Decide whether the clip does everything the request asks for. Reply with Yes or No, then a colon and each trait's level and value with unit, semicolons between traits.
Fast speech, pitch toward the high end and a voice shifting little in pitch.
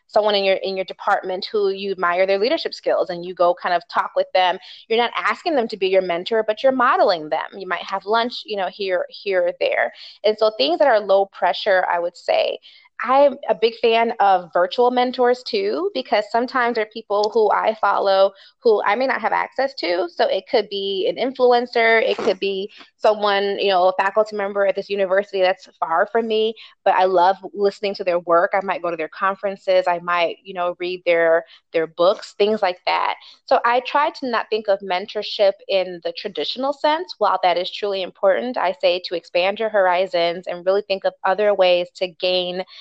No: fast, 215 wpm; high, 195 Hz; average, 3.7 semitones